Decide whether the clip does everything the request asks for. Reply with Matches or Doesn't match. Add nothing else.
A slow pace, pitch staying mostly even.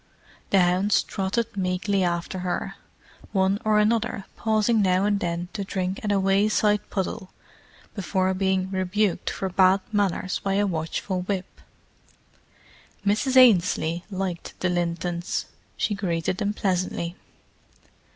Matches